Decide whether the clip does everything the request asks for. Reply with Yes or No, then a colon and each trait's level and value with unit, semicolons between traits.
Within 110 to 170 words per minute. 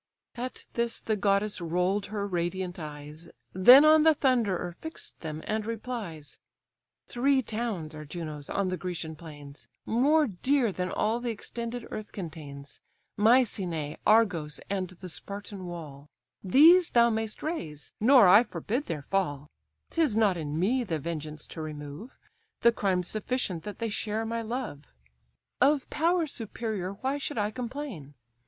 Yes: average, 150 wpm